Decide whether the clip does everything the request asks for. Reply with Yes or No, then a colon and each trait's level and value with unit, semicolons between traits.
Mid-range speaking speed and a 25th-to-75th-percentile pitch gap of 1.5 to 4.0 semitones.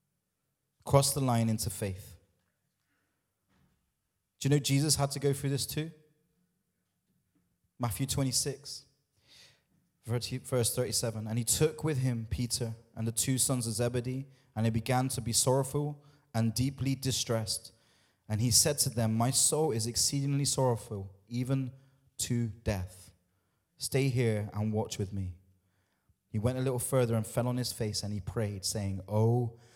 Yes: average, 150 wpm; average, 3.7 semitones